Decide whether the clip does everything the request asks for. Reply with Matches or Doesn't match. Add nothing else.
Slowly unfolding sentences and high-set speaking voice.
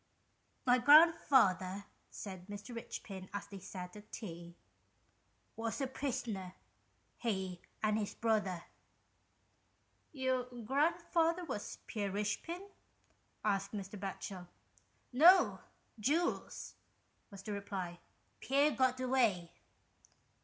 Matches